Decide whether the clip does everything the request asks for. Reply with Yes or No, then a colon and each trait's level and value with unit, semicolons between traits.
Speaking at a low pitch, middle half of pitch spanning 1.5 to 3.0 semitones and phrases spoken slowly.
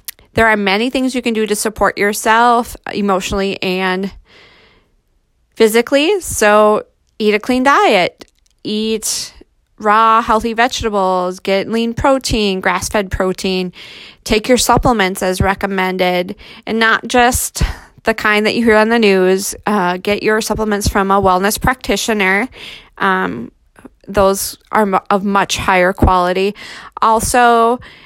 No: high, 210 Hz; average, 2.7 semitones; slow, 130 wpm